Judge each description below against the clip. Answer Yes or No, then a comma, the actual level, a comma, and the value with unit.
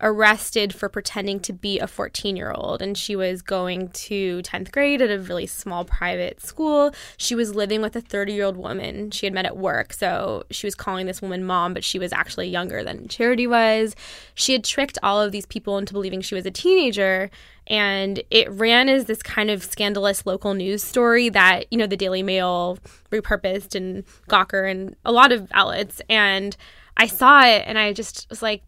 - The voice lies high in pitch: Yes, high, 205 Hz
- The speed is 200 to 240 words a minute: Yes, fast, 205 wpm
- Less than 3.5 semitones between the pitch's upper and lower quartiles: Yes, average, 2.8 semitones